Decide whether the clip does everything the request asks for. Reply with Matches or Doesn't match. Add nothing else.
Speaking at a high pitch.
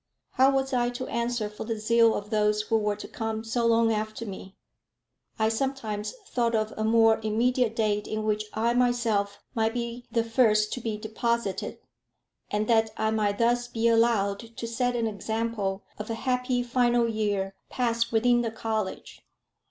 Matches